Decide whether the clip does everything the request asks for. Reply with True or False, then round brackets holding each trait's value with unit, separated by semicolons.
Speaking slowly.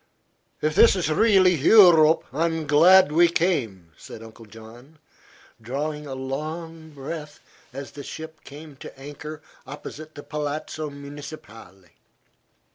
True (125 wpm)